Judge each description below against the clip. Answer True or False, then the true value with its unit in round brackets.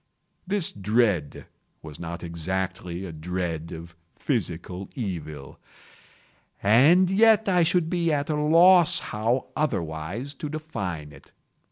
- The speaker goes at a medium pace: False (115 wpm)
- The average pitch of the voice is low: True (100 Hz)